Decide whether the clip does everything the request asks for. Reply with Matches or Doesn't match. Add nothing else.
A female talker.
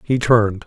Doesn't match